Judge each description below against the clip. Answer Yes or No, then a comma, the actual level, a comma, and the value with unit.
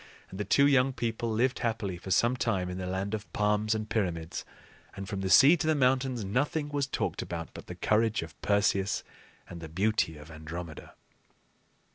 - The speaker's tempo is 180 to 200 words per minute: Yes, average, 190 wpm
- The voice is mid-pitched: No, low, 105 Hz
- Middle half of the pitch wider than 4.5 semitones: Yes, average, 4.9 semitones